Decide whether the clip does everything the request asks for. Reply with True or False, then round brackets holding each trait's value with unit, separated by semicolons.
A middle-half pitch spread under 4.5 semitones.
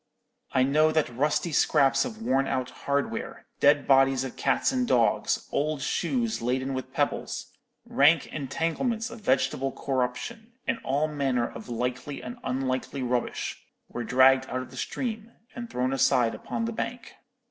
False (5.1 semitones)